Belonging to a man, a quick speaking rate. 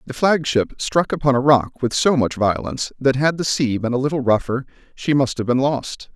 Yes: male; fast, 235 wpm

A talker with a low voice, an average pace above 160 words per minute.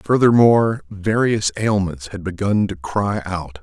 No: very low, 95 Hz; slow, 135 wpm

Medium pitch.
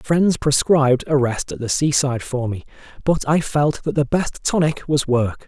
Yes: medium, 145 Hz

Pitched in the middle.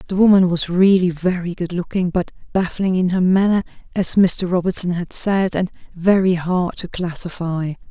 Yes: medium, 180 Hz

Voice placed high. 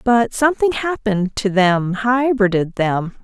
Yes: high, 220 Hz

